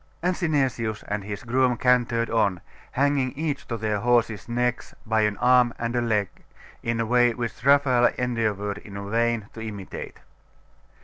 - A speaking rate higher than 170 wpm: No, average, 160 wpm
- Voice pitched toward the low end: Yes, low, 115 Hz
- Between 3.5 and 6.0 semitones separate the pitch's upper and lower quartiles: No, narrow, 2.6 semitones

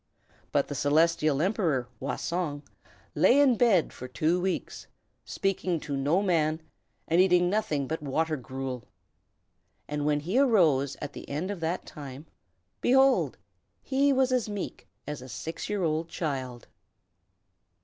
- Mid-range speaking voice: Yes, medium, 160 Hz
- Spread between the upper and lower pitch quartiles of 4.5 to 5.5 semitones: Yes, average, 5.1 semitones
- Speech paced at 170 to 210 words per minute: No, average, 145 wpm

